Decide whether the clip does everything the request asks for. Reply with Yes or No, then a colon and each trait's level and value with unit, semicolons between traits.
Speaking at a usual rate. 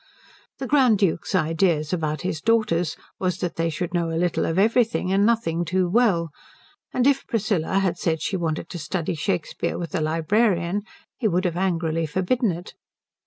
Yes: average, 175 wpm